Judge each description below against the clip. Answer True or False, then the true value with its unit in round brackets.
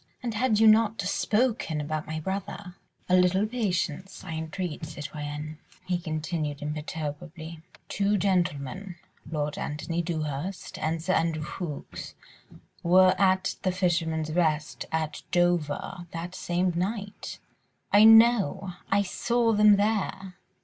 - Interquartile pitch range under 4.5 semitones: True (4.0 semitones)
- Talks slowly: True (125 wpm)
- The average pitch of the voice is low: False (175 Hz)